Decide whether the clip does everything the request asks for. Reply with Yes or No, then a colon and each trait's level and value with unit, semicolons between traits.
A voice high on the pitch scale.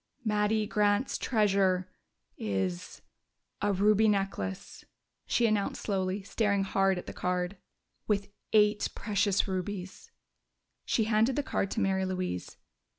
Yes: high, 200 Hz